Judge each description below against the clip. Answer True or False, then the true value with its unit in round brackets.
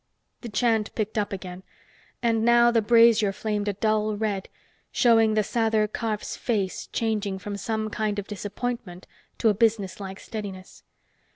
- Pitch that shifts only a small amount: True (1.9 semitones)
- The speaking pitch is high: True (215 Hz)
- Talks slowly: False (150 wpm)